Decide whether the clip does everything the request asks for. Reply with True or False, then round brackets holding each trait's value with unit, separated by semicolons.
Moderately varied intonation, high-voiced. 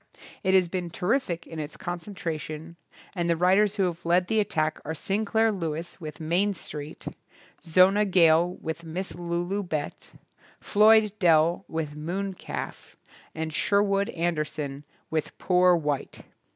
False (3.4 semitones; 175 Hz)